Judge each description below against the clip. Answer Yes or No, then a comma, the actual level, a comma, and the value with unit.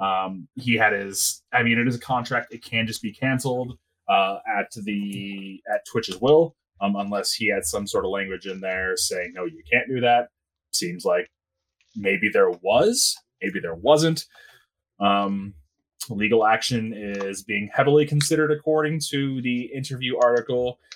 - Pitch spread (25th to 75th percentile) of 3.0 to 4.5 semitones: No, average, 5.0 semitones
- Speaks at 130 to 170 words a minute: Yes, average, 165 wpm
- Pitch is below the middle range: Yes, low, 120 Hz